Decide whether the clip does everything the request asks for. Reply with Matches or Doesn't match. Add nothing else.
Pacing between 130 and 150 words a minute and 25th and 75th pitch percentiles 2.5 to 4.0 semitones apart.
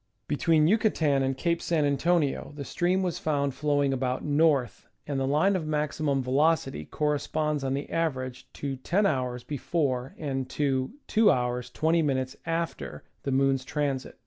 Matches